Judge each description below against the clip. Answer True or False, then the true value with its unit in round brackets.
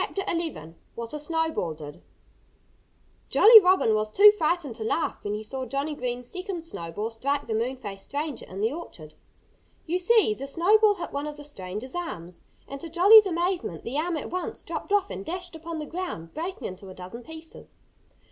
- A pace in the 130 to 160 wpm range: False (185 wpm)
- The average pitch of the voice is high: True (295 Hz)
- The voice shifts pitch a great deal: True (8.1 semitones)